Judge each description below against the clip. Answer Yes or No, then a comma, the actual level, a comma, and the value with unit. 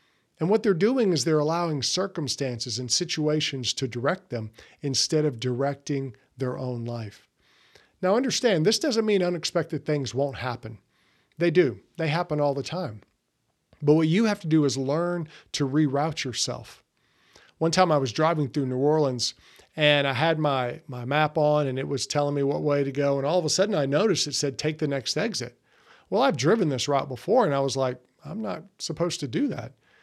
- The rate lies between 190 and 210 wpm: Yes, average, 200 wpm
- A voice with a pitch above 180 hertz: No, medium, 145 Hz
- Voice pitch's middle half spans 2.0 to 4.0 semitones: Yes, average, 3.4 semitones